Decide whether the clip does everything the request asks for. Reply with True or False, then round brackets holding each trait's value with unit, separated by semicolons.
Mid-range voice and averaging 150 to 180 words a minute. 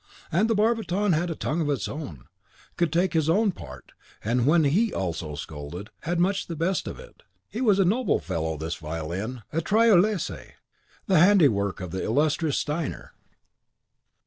True (160 Hz; 170 wpm)